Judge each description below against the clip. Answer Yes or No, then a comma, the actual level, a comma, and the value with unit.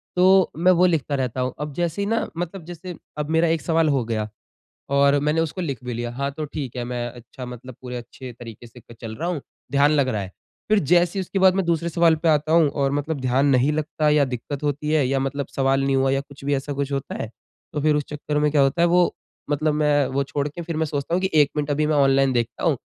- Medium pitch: Yes, medium, 145 Hz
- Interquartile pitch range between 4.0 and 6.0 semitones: No, average, 3.2 semitones